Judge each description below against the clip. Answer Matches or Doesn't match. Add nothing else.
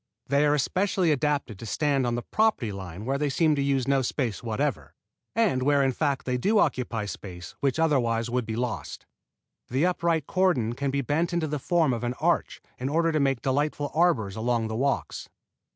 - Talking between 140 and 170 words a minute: Doesn't match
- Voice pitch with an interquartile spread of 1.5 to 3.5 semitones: Doesn't match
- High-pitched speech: Doesn't match